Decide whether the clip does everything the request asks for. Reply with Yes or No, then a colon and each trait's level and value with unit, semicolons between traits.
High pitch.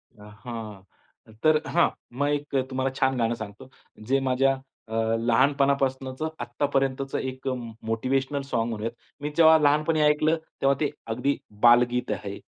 No: low, 130 Hz